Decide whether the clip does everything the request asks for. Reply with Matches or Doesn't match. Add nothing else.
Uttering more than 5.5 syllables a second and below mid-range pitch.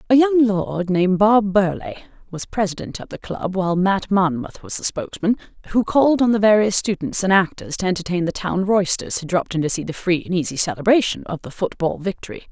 Doesn't match